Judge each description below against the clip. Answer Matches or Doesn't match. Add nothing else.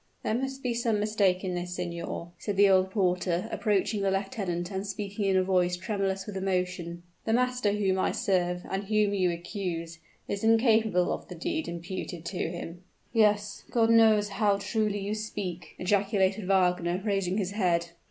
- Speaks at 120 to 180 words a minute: Matches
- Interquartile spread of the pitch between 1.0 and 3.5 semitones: Matches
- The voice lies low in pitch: Doesn't match